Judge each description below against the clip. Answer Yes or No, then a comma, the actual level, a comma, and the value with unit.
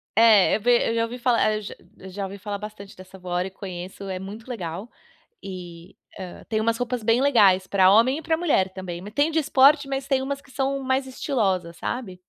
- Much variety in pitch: Yes, wide, 5.7 semitones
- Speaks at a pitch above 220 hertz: No, high, 215 Hz